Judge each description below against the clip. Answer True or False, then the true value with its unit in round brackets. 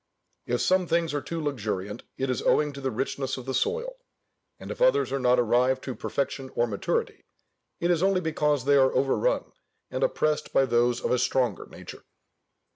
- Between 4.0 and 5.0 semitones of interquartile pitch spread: True (4.6 semitones)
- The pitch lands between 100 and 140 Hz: True (135 Hz)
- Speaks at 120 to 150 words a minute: False (190 wpm)